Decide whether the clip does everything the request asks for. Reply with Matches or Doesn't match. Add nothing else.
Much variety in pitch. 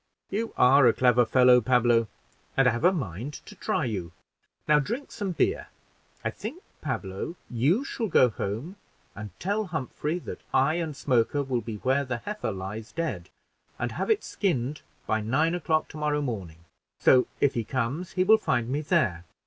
Matches